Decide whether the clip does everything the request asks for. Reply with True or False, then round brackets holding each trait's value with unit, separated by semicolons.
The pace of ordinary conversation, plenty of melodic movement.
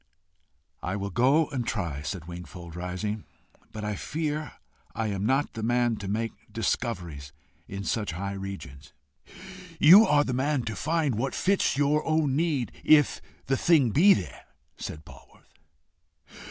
True (150 wpm; 7.1 semitones)